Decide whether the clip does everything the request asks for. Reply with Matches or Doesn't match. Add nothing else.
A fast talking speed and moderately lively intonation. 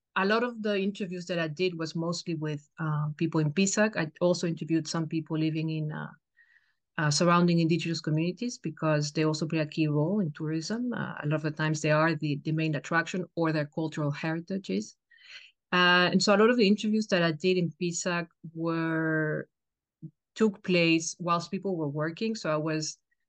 Doesn't match